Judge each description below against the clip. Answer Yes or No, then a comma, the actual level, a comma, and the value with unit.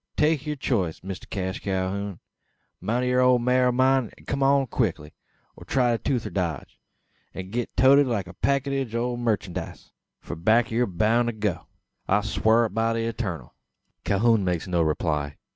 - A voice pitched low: Yes, low, 115 Hz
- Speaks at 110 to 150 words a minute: No, average, 175 wpm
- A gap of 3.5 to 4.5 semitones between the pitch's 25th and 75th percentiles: No, average, 5.0 semitones